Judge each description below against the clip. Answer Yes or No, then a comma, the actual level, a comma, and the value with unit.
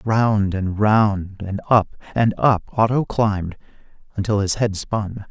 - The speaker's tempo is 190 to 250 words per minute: No, average, 145 wpm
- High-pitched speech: No, low, 105 Hz